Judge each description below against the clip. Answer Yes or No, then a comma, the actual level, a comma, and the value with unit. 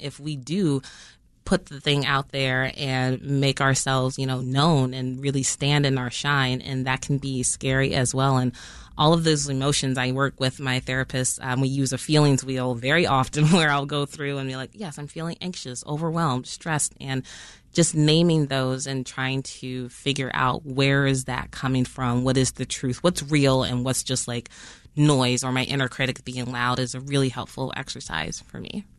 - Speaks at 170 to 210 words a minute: Yes, average, 200 wpm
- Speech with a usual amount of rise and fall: No, narrow, 1.8 semitones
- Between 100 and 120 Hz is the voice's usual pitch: No, low, 135 Hz